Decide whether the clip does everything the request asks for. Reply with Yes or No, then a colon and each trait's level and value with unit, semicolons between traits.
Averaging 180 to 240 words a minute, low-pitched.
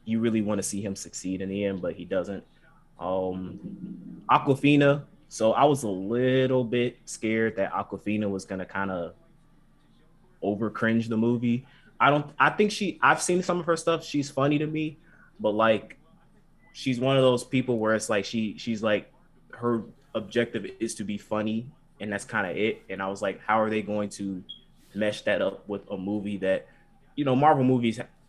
Yes: average, 195 wpm; low, 115 Hz